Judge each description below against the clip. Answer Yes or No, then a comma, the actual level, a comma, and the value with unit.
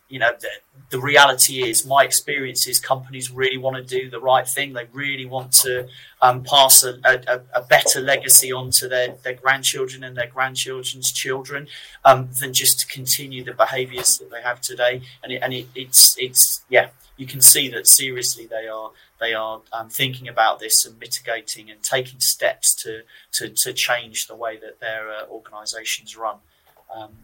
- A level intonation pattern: Yes, narrow, 1.5 semitones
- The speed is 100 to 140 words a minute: No, average, 185 wpm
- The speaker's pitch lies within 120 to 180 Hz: Yes, low, 130 Hz